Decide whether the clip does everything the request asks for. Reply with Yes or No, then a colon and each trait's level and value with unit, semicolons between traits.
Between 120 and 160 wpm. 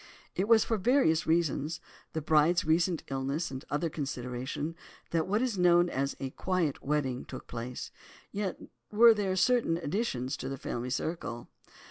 Yes: average, 155 wpm